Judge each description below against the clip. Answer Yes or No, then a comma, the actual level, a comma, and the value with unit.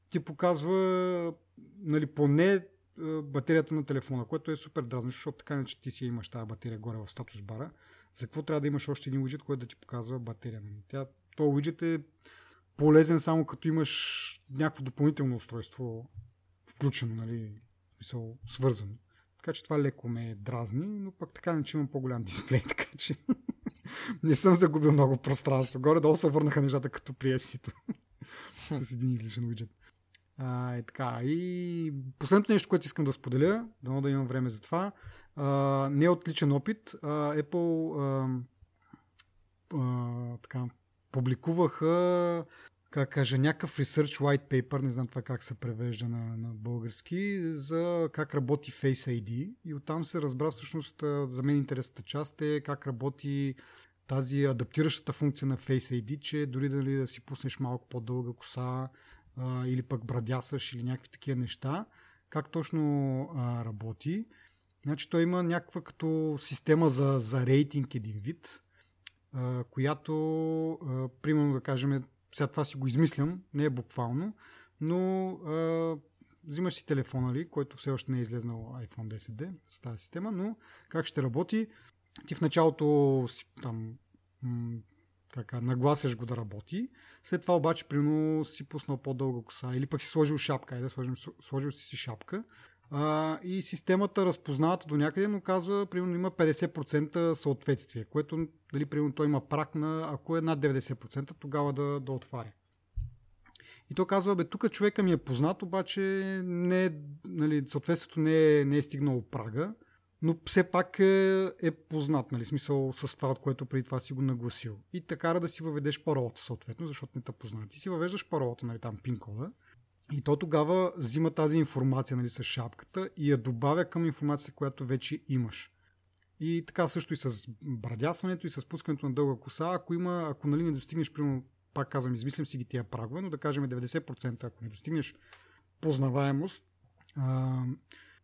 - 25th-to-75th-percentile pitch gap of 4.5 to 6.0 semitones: No, average, 4.1 semitones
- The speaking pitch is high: No, medium, 140 Hz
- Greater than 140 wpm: Yes, average, 160 wpm